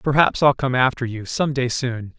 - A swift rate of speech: Yes, fast, 220 wpm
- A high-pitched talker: No, low, 130 Hz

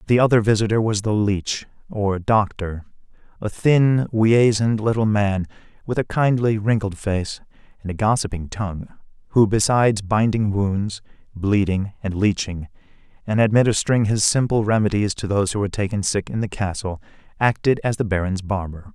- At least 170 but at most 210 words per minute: No, average, 150 wpm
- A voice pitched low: Yes, low, 105 Hz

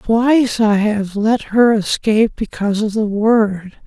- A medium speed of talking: Yes, average, 155 wpm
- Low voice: No, high, 215 Hz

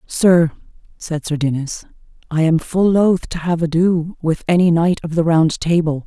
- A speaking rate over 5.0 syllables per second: No, 4.5 syllables/s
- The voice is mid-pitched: Yes, medium, 165 Hz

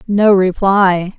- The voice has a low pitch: No, high, 195 Hz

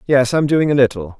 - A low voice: Yes, low, 130 Hz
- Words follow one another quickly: Yes, fast, 300 wpm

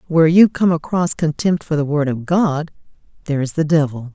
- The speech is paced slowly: No, average, 200 wpm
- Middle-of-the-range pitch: Yes, medium, 155 Hz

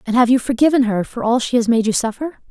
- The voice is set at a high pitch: Yes, high, 240 Hz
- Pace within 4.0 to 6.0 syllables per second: No, 6.5 syllables/s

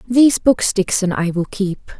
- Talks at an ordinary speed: Yes, average, 180 wpm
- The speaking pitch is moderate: No, high, 205 Hz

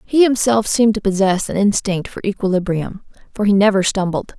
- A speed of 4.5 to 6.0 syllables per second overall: Yes, 5.5 syllables/s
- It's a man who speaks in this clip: No, female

